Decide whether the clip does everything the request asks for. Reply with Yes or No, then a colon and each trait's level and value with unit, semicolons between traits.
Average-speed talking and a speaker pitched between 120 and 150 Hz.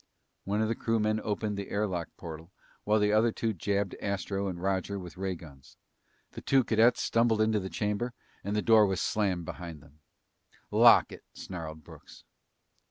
No: average, 175 wpm; low, 100 Hz